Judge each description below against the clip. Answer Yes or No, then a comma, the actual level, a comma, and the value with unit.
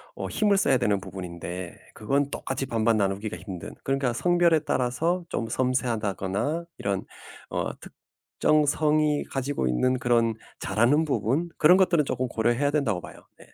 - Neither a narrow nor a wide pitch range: No, wide, 6.1 semitones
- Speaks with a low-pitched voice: Yes, low, 125 Hz